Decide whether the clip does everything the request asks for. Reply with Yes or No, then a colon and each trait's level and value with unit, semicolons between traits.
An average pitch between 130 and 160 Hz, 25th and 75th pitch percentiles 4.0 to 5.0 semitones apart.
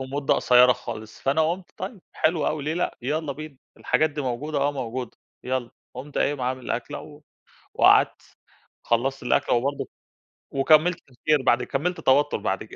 No: medium, 140 Hz; average, 3.3 semitones